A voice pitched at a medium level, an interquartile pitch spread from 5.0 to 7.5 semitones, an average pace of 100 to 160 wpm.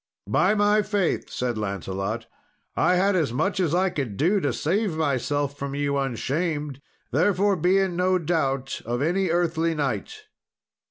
Yes: medium, 160 Hz; wide, 5.4 semitones; average, 155 wpm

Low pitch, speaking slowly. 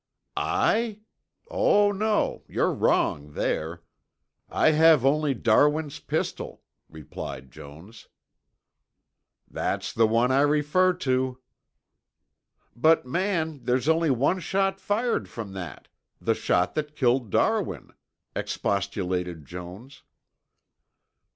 Yes: low, 130 Hz; slow, 100 wpm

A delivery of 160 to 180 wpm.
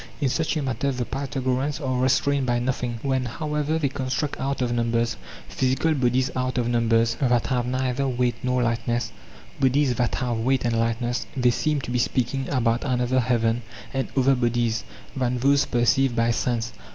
Yes: average, 175 wpm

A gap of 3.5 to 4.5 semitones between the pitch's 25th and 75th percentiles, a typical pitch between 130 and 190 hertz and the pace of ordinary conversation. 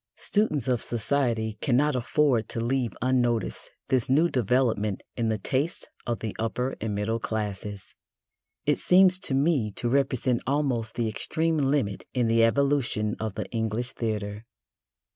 No: average, 3.8 semitones; low, 120 Hz; average, 145 wpm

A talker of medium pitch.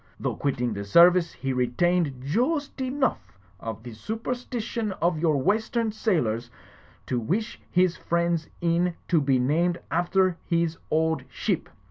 Yes: medium, 170 Hz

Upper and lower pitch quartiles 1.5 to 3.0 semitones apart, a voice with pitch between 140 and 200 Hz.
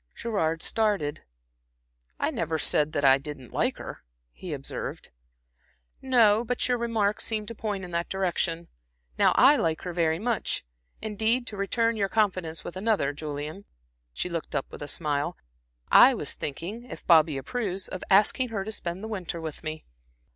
No: wide, 5.6 semitones; medium, 185 Hz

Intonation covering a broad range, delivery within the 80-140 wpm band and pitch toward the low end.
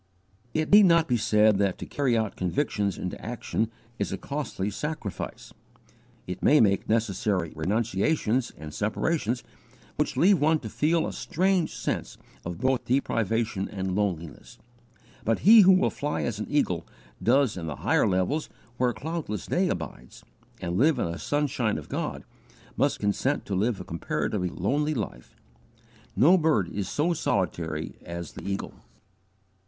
No: wide, 7.7 semitones; average, 155 wpm; low, 110 Hz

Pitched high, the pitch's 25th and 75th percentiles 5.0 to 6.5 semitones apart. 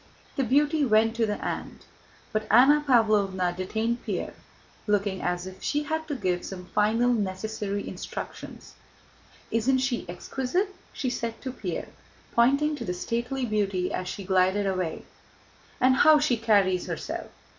Yes: high, 220 Hz; wide, 5.5 semitones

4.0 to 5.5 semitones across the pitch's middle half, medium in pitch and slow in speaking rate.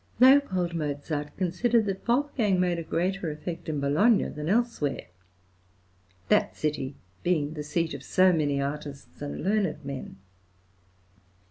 Yes: average, 4.8 semitones; medium, 165 Hz; slow, 130 wpm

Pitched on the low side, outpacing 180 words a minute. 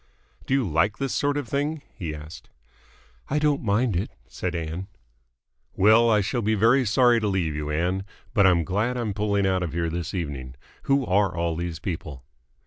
Yes: very low, 95 Hz; average, 190 wpm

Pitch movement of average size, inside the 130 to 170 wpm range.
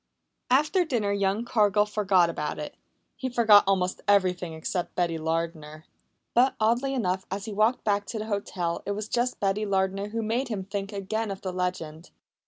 No: average, 3.2 semitones; average, 180 wpm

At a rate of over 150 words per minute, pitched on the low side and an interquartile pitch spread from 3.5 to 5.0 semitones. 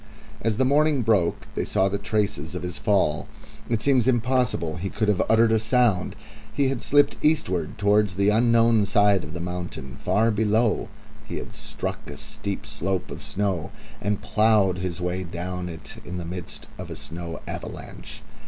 Yes: average, 175 wpm; low, 100 Hz; average, 4.1 semitones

